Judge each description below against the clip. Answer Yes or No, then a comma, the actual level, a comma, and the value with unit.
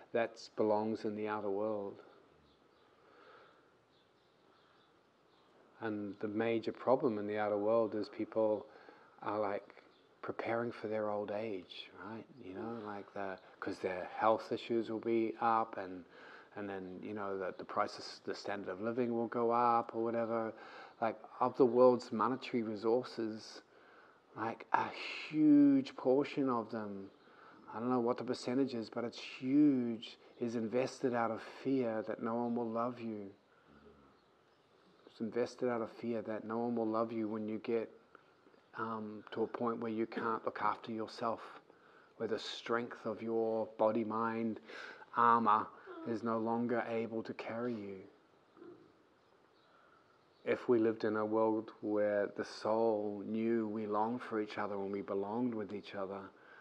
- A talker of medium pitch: No, low, 115 Hz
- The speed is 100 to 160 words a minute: Yes, average, 155 wpm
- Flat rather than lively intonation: Yes, narrow, 1.8 semitones